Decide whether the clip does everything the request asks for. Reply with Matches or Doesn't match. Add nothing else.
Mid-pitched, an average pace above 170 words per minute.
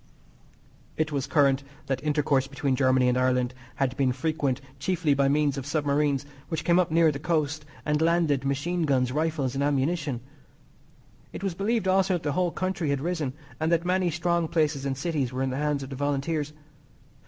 Matches